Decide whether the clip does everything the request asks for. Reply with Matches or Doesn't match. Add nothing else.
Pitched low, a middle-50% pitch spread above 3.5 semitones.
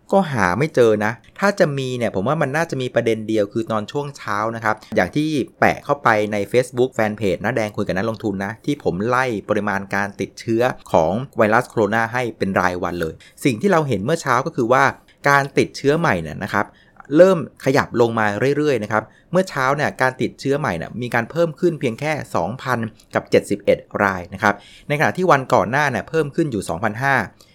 Matches